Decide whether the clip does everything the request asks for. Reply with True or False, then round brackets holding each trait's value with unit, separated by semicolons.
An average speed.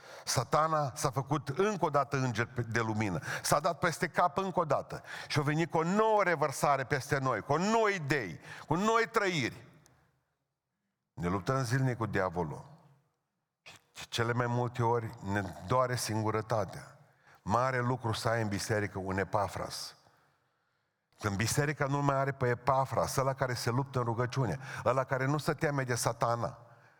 True (160 wpm)